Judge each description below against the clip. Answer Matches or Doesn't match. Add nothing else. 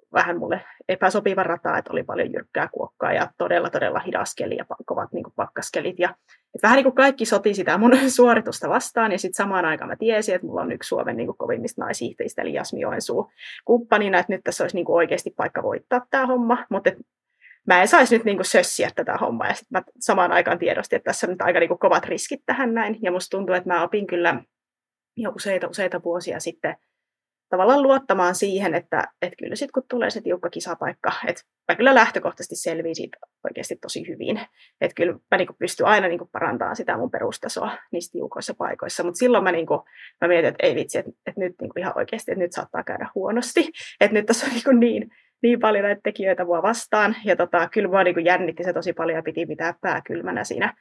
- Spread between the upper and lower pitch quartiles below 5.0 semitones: Doesn't match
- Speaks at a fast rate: Matches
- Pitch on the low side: Doesn't match